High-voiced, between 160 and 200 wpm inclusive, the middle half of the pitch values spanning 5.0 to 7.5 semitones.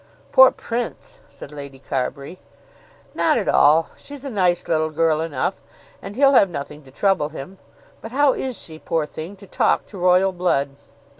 No: medium, 175 Hz; average, 170 wpm; average, 5.3 semitones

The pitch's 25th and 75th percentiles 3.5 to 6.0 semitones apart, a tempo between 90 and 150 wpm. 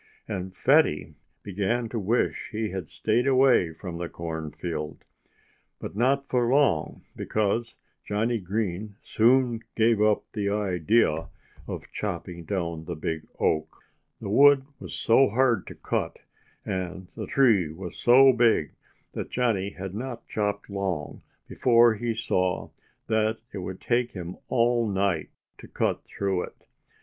Yes: average, 4.5 semitones; average, 140 wpm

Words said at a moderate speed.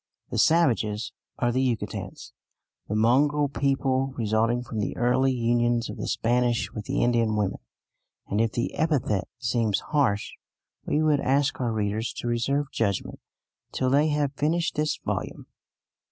Yes: average, 150 wpm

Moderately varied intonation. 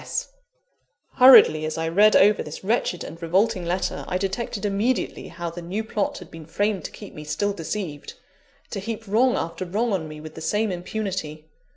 Yes: average, 4.4 semitones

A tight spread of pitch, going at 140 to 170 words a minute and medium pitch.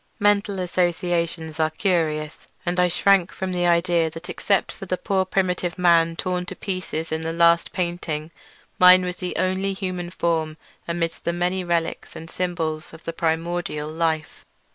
Yes: narrow, 1.9 semitones; average, 160 wpm; medium, 175 Hz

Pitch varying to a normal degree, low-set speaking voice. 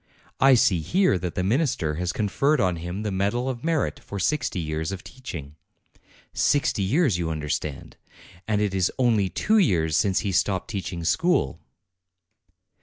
No: wide, 6.7 semitones; low, 100 Hz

